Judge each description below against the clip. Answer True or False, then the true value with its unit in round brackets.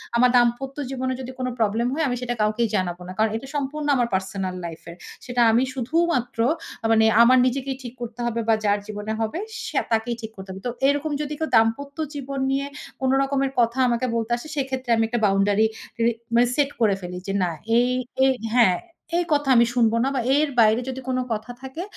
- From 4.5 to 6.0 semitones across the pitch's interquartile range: False (3.3 semitones)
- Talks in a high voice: True (240 Hz)